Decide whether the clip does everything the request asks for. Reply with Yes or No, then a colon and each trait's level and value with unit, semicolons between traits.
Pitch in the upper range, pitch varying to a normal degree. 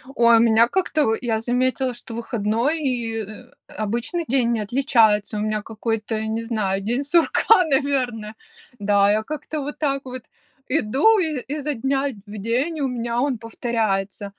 Yes: high, 235 Hz; average, 3.9 semitones